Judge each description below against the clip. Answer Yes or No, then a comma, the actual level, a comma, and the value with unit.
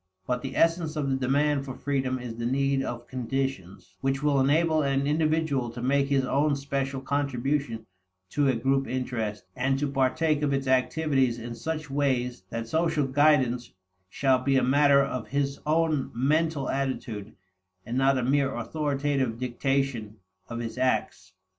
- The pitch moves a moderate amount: No, narrow, 2.3 semitones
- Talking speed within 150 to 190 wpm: Yes, average, 160 wpm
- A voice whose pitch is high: No, low, 135 Hz